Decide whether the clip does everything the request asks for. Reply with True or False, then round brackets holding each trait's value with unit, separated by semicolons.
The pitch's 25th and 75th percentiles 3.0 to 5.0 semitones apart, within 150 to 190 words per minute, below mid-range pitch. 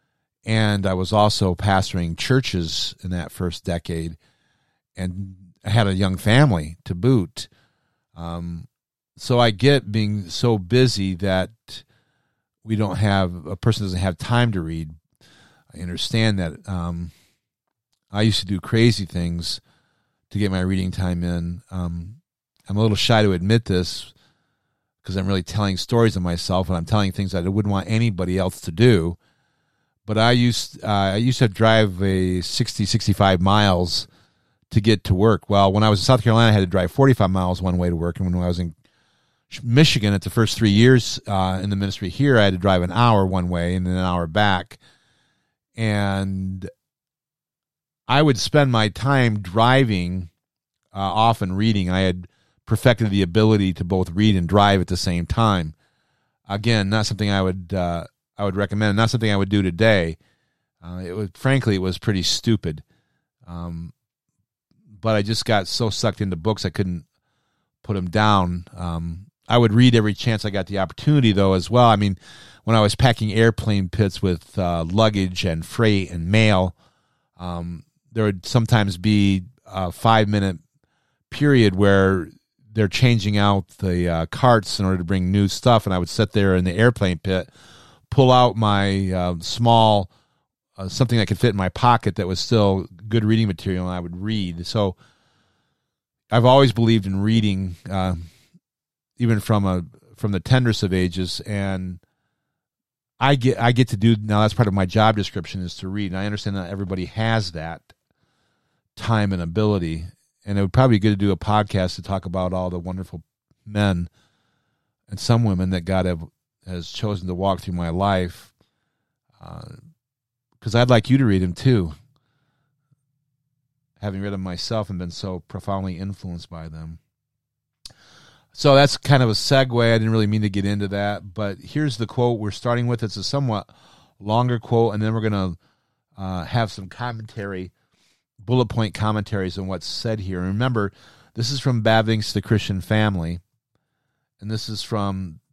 True (3.8 semitones; 180 wpm; 100 Hz)